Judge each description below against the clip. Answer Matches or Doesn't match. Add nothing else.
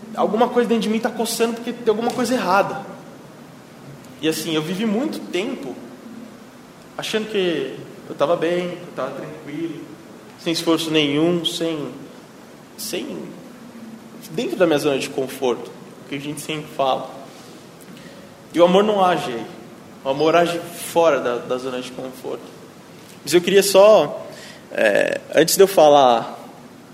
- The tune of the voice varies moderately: Doesn't match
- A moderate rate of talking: Matches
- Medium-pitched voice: Matches